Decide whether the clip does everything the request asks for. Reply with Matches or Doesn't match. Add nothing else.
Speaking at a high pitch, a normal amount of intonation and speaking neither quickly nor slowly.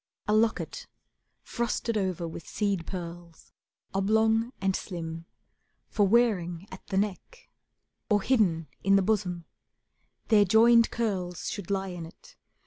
Doesn't match